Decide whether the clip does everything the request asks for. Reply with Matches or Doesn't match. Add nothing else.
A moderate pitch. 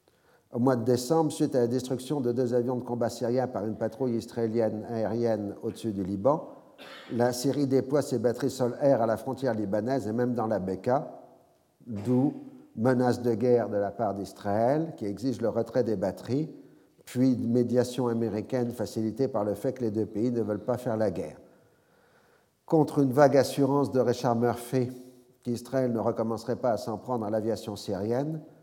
Doesn't match